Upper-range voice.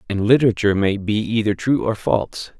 No: low, 105 Hz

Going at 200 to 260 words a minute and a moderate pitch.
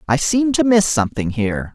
Yes: fast, 205 wpm; medium, 155 Hz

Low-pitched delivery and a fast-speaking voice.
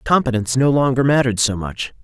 No: low, 125 Hz; average, 175 wpm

